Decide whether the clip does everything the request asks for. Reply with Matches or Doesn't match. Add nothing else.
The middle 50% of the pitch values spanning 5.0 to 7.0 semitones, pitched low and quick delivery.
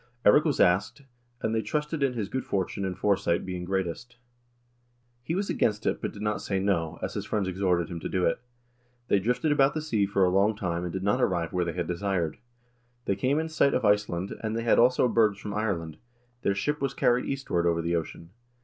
Matches